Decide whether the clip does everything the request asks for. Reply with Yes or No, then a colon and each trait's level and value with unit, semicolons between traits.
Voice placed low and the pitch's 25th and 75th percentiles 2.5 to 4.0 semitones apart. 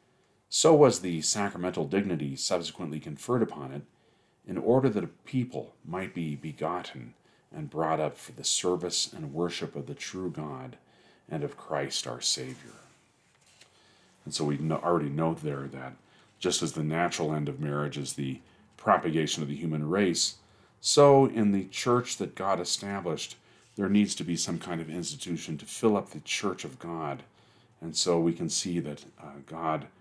No: very low, 85 Hz; average, 4.8 semitones